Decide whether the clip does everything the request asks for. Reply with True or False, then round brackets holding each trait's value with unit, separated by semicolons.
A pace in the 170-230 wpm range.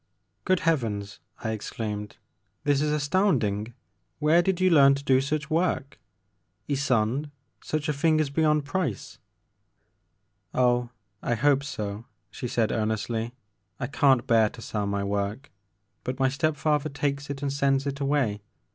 False (155 wpm)